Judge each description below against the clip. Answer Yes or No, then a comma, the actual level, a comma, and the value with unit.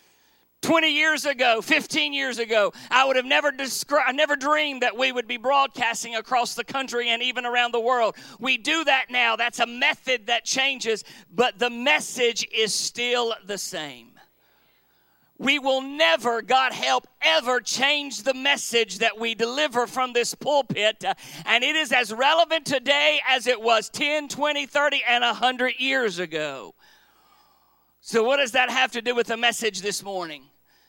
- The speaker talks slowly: No, average, 165 wpm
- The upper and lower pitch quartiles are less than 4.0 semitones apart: Yes, average, 3.6 semitones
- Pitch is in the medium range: No, very high, 255 Hz